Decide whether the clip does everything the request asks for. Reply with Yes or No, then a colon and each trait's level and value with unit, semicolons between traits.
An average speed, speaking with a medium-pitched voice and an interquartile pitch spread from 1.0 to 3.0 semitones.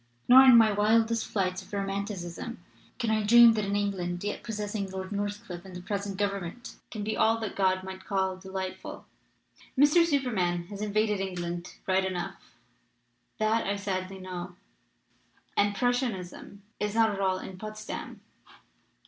No: average, 150 wpm; high, 200 Hz; narrow, 2.6 semitones